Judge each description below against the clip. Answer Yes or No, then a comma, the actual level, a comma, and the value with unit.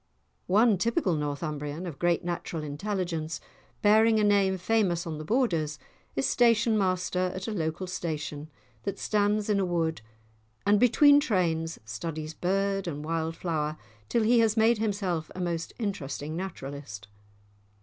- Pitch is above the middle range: No, medium, 180 Hz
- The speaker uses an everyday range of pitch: Yes, average, 4.7 semitones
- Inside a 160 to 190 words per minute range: No, average, 145 wpm